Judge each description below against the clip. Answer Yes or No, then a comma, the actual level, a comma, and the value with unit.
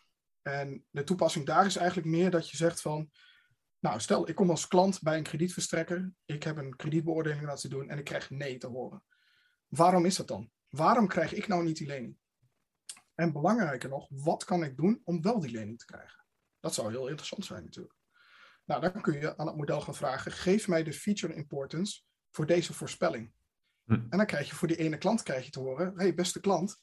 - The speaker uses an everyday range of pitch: Yes, average, 3.7 semitones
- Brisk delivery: Yes, fast, 210 wpm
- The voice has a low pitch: No, medium, 165 Hz